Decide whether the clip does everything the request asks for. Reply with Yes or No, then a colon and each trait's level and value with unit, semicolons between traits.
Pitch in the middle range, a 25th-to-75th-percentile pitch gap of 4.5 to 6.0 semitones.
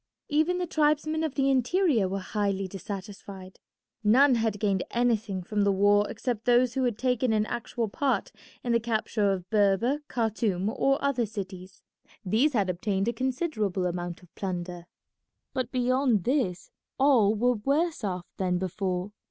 No: high, 220 Hz; average, 4.9 semitones